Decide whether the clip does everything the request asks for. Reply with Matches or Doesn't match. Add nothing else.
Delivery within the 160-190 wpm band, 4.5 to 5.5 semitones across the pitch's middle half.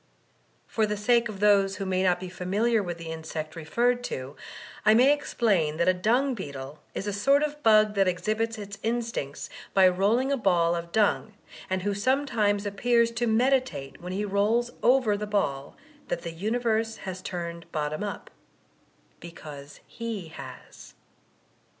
Matches